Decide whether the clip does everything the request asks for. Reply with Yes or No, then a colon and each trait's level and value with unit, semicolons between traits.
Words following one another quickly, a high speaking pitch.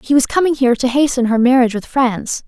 Yes: fast, 240 wpm; very high, 255 Hz